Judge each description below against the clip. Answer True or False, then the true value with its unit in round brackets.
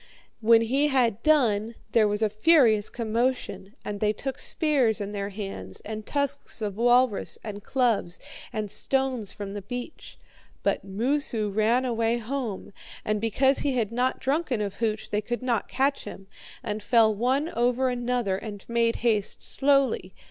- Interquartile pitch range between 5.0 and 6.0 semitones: False (3.6 semitones)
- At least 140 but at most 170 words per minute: True (160 wpm)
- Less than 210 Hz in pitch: False (230 Hz)